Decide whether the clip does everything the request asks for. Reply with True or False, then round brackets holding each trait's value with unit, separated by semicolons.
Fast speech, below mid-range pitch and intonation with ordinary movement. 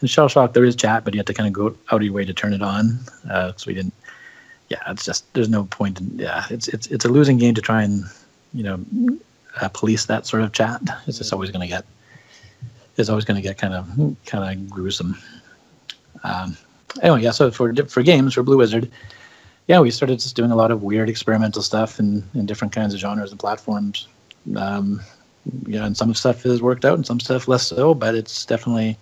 True (235 wpm; 110 Hz; 3.1 semitones)